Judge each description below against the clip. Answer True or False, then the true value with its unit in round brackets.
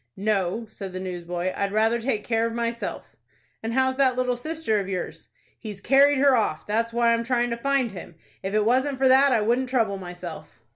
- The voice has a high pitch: True (230 Hz)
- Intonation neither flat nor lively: True (4.4 semitones)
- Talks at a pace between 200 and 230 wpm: True (205 wpm)